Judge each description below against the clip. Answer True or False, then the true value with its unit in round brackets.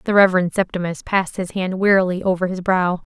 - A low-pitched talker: False (185 Hz)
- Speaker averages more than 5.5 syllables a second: True (6.2 syllables/s)